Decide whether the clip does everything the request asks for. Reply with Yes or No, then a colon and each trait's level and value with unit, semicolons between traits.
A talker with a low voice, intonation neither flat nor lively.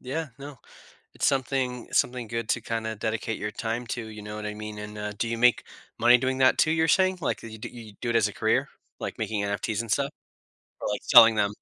Yes: low, 115 Hz; average, 3.0 semitones